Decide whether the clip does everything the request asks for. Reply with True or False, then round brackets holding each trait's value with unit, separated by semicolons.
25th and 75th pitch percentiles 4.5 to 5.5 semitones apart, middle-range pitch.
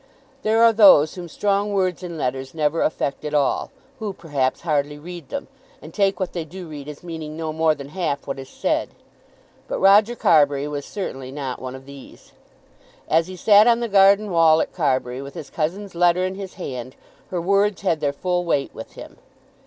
True (5.1 semitones; 165 Hz)